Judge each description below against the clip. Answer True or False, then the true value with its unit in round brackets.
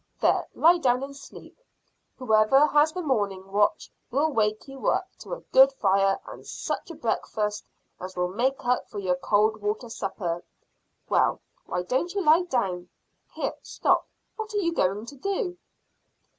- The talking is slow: False (165 wpm)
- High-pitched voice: True (240 Hz)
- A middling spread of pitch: False (7.0 semitones)